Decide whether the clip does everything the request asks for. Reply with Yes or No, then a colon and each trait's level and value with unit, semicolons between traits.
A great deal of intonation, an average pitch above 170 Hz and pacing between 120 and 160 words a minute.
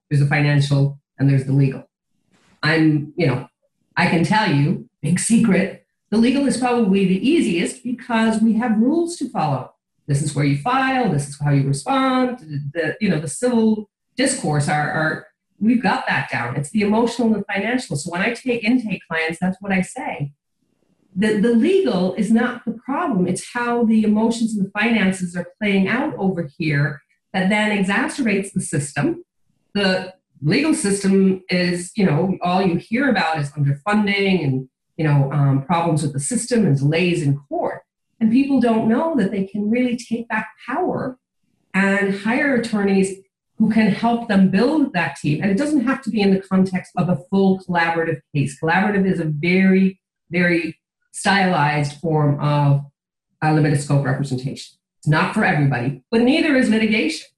No: wide, 6.5 semitones; high, 190 Hz; average, 175 wpm